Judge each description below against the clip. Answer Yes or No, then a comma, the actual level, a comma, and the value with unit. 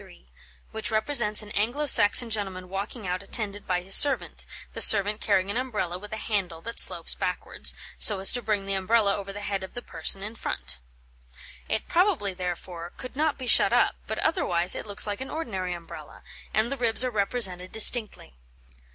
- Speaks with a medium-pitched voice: No, high, 205 Hz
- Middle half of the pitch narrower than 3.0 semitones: No, average, 3.7 semitones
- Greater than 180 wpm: Yes, average, 190 wpm